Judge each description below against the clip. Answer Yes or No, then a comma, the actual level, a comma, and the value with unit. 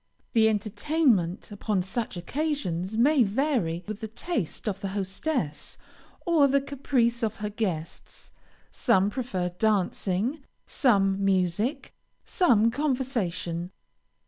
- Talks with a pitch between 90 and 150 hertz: No, high, 215 Hz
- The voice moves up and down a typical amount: No, wide, 5.8 semitones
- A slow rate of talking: Yes, slow, 110 wpm